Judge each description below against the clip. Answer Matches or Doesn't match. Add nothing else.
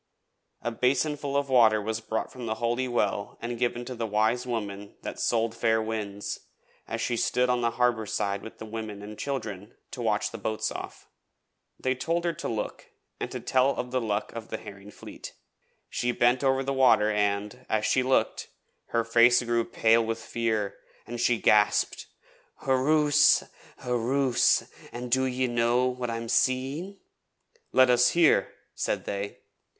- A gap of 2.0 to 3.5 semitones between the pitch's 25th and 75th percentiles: Matches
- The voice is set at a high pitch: Doesn't match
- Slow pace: Doesn't match